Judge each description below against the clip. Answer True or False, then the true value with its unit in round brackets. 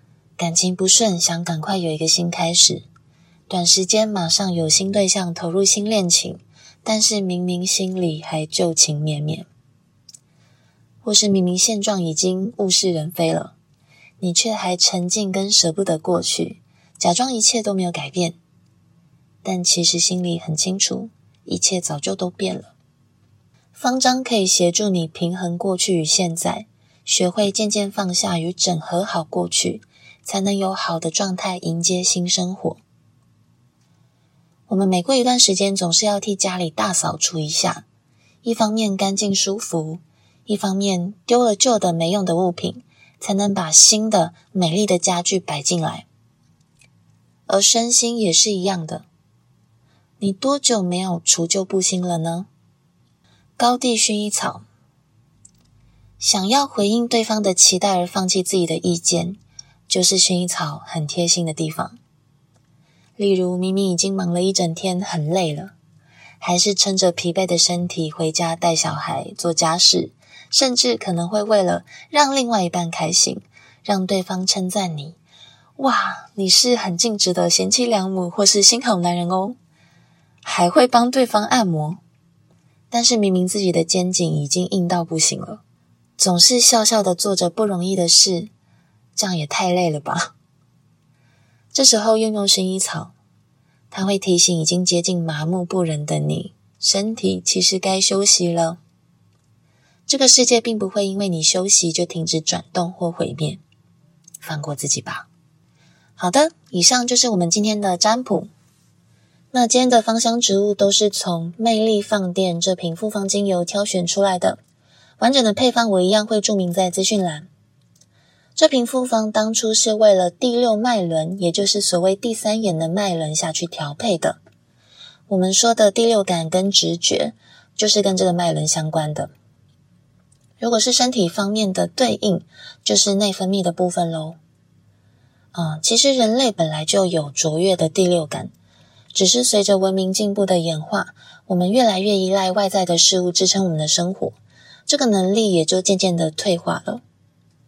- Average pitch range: True (3.7 semitones)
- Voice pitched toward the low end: False (185 Hz)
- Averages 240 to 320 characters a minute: False (230 characters per minute)